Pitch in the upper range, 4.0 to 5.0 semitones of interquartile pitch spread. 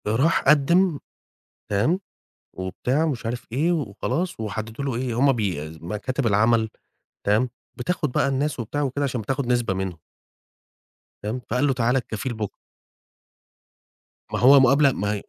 No: low, 125 Hz; average, 4.5 semitones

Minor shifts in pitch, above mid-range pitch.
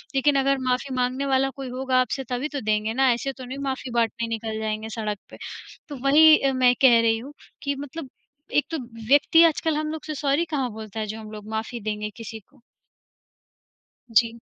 No: average, 3.8 semitones; very high, 255 Hz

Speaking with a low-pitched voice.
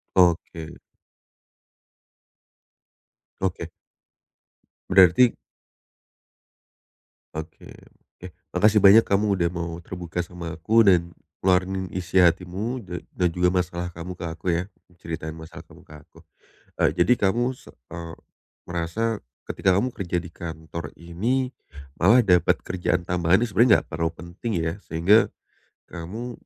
Yes: very low, 90 Hz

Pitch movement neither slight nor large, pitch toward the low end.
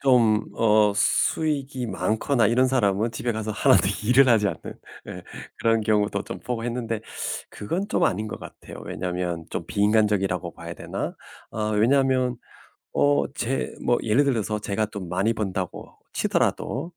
Yes: average, 3.3 semitones; low, 110 Hz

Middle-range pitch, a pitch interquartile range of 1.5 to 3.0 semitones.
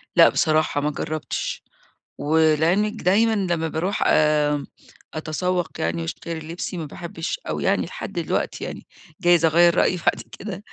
Yes: medium, 165 Hz; narrow, 2.6 semitones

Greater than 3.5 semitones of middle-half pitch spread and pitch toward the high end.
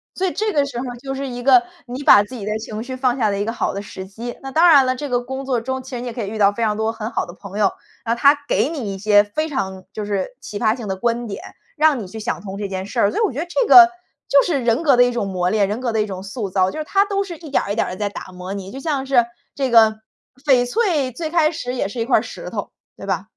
Yes: average, 5.1 semitones; high, 240 Hz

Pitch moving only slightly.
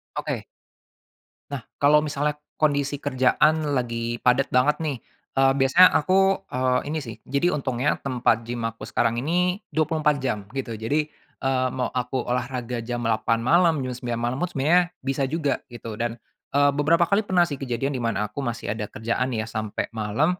No: average, 3.7 semitones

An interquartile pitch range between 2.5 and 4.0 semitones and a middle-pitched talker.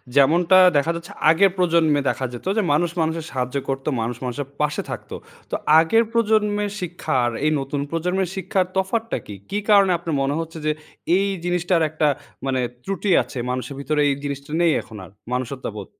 No: average, 5.2 semitones; medium, 160 Hz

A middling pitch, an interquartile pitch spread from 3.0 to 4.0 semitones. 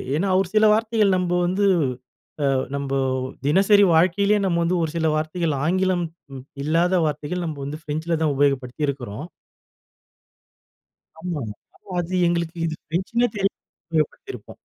Yes: medium, 170 Hz; average, 3.6 semitones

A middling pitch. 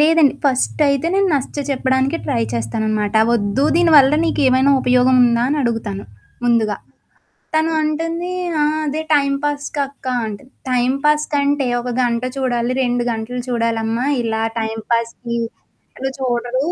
No: very high, 255 Hz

